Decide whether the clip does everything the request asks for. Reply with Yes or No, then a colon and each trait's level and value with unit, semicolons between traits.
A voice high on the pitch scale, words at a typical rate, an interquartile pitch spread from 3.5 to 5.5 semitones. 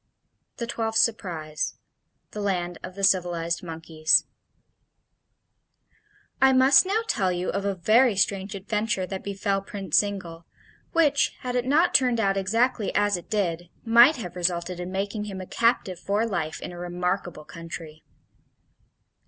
Yes: high, 195 Hz; average, 145 wpm; average, 4.2 semitones